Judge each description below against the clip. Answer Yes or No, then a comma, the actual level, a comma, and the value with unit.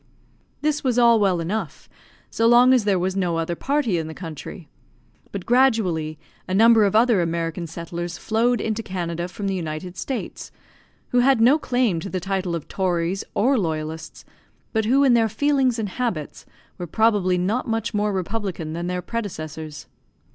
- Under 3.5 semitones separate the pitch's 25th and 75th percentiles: No, average, 5.3 semitones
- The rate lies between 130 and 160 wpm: No, average, 170 wpm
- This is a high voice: Yes, high, 195 Hz